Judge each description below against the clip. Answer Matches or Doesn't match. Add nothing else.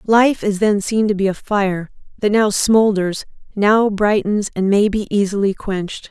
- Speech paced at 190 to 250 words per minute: Doesn't match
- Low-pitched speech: Doesn't match